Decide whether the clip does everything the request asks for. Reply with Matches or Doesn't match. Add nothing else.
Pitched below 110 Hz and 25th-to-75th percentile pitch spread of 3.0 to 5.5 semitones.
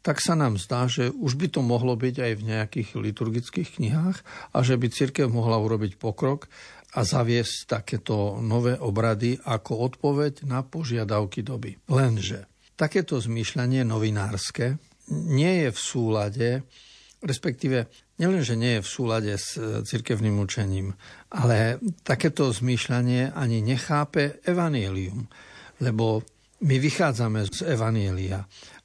Doesn't match